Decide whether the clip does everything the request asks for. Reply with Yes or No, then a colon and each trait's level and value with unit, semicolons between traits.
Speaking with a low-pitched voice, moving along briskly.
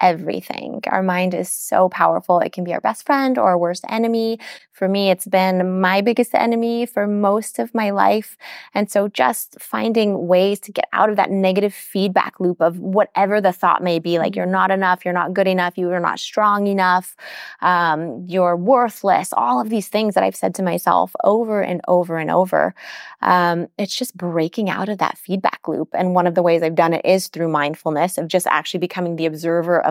No: medium, 185 Hz; fast, 210 wpm